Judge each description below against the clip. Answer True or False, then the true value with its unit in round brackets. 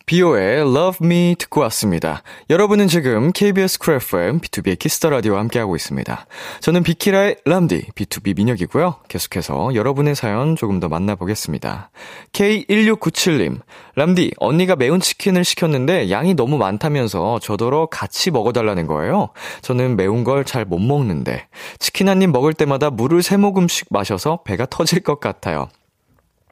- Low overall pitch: False (155 Hz)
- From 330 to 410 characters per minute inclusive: True (345 characters per minute)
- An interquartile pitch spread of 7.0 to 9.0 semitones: True (7.8 semitones)